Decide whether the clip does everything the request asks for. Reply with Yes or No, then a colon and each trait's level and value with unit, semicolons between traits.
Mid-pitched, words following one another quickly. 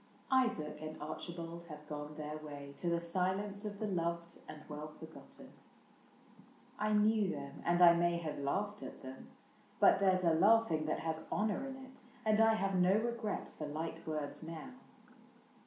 No: medium, 170 Hz; average, 170 wpm